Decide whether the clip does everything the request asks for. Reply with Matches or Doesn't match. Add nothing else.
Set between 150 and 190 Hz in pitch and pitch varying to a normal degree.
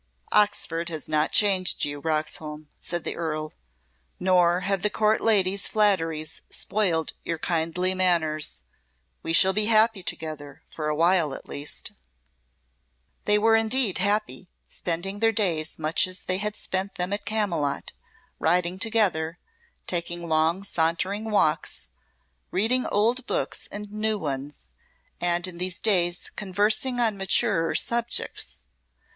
Matches